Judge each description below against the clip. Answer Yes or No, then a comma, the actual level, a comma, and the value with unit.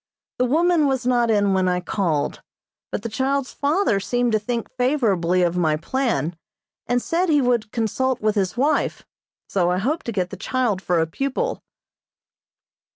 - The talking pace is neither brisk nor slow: Yes, average, 170 wpm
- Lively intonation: Yes, wide, 5.9 semitones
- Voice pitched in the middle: No, high, 230 Hz